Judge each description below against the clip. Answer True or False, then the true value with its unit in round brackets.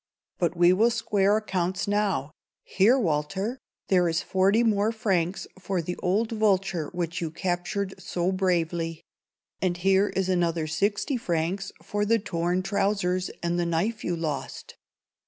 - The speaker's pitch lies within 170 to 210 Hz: True (185 Hz)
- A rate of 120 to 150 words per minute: True (140 wpm)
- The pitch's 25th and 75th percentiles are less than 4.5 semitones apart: True (2.8 semitones)